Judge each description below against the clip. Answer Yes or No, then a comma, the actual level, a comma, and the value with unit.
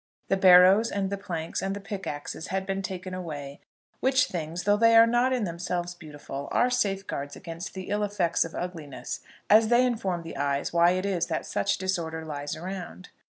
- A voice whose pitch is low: No, medium, 185 Hz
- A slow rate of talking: No, average, 190 wpm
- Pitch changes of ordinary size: Yes, average, 3.4 semitones